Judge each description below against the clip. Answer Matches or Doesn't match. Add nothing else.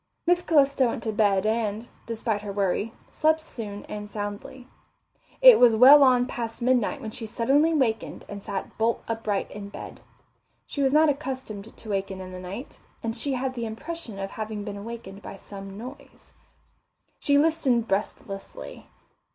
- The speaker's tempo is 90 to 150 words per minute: Doesn't match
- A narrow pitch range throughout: Doesn't match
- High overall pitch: Matches